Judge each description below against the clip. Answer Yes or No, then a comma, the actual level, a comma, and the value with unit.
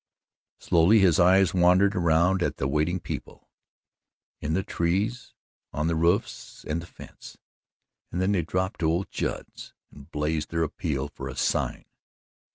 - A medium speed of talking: Yes, average, 155 wpm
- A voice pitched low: Yes, very low, 85 Hz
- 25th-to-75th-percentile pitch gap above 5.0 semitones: No, average, 2.9 semitones